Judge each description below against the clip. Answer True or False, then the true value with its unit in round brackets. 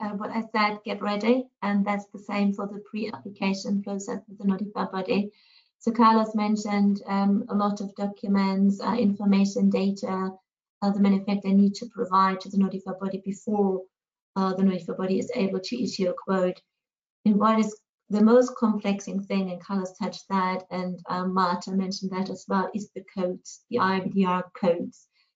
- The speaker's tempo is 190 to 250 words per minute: False (175 wpm)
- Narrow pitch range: True (1.9 semitones)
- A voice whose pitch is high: True (200 Hz)